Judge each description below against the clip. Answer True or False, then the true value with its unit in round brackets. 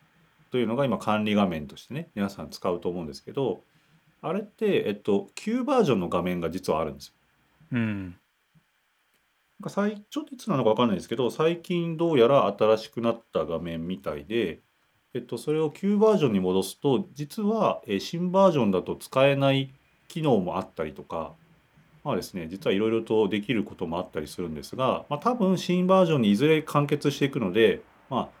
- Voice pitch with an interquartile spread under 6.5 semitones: False (8.5 semitones)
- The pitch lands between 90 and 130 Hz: False (140 Hz)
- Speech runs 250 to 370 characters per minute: True (340 characters per minute)